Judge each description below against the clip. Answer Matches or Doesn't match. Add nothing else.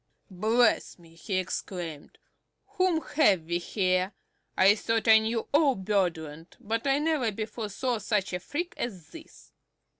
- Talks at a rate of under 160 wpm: Matches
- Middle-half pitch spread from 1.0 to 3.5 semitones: Doesn't match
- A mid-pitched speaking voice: Doesn't match